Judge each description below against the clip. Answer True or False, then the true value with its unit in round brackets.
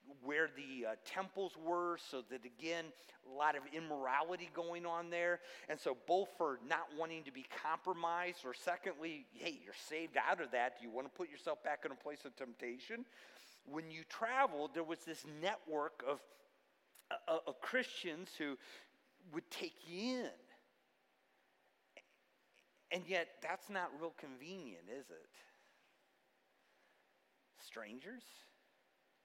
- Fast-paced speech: False (140 wpm)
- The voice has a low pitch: False (165 Hz)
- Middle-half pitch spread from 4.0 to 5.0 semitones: False (3.4 semitones)